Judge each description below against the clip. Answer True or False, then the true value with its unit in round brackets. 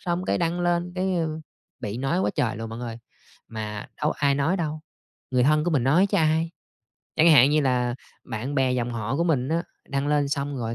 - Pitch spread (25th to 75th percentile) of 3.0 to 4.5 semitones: False (5.2 semitones)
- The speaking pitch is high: False (145 Hz)